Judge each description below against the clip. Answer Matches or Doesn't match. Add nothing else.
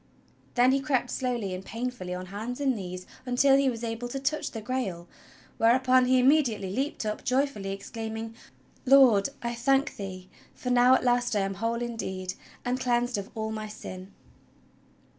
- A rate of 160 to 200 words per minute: Matches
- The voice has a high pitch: Matches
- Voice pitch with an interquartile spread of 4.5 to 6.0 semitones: Doesn't match